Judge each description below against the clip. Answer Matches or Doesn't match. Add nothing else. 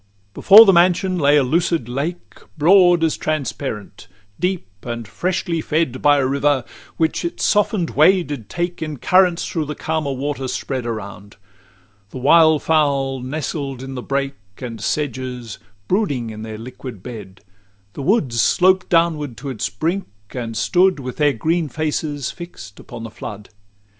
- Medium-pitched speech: Matches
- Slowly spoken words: Doesn't match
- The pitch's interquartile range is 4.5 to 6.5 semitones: Matches